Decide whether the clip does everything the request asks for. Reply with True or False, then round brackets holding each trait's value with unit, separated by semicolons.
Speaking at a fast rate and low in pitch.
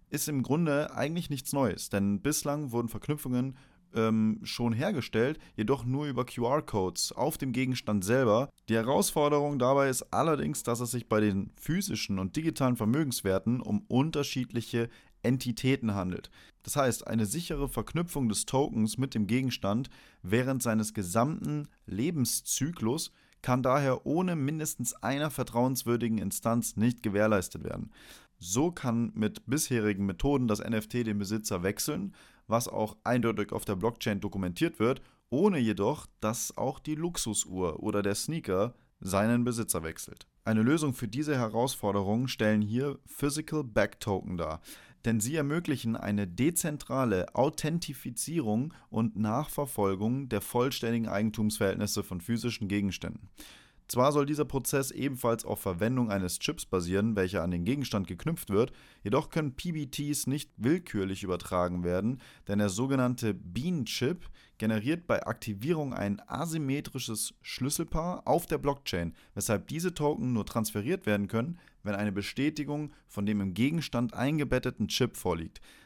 False (135 wpm; 120 Hz)